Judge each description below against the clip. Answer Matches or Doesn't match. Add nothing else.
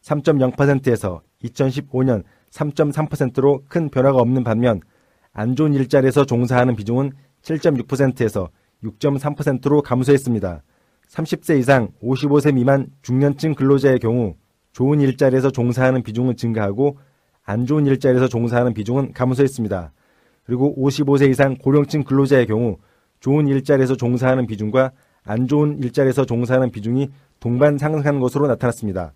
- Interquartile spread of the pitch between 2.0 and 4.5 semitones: Matches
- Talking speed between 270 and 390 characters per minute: Matches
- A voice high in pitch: Doesn't match